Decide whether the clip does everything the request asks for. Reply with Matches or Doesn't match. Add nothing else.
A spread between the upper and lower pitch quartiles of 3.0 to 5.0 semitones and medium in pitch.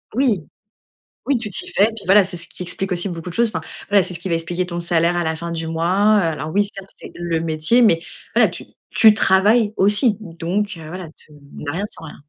Matches